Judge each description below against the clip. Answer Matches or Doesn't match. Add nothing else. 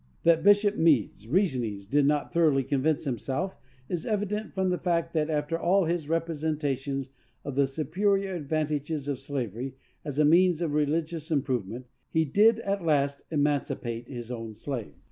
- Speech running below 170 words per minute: Matches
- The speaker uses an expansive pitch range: Doesn't match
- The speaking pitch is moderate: Matches